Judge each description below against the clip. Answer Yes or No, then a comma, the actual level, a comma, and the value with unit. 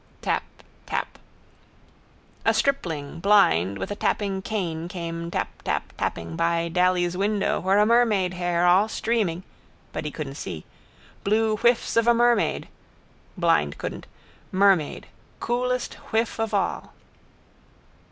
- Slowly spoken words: Yes, slow, 120 wpm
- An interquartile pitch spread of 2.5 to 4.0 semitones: No, average, 4.5 semitones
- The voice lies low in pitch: No, medium, 185 Hz